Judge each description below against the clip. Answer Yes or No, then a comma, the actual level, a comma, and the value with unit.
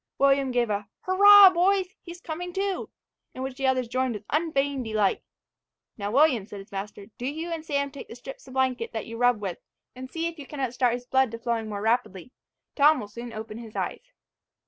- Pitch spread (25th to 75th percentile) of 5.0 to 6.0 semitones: Yes, average, 5.3 semitones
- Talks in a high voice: Yes, very high, 260 Hz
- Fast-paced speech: Yes, fast, 215 wpm